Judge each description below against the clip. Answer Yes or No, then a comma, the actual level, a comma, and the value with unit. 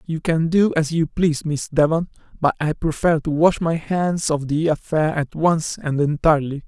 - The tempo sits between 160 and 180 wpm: No, average, 200 wpm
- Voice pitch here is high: No, medium, 155 Hz